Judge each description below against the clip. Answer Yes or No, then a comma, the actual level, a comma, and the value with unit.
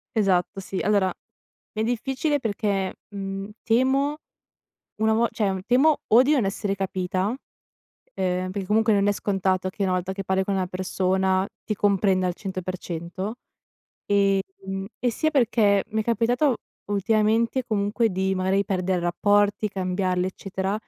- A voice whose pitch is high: Yes, high, 200 Hz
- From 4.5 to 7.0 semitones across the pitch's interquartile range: No, average, 2.7 semitones